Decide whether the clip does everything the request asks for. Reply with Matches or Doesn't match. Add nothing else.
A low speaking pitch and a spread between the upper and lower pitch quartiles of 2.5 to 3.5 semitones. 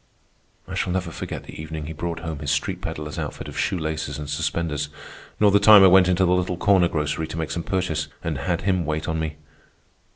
Matches